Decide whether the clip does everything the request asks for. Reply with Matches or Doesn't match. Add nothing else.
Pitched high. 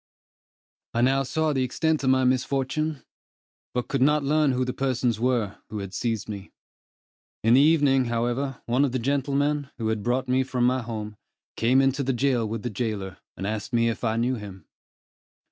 Doesn't match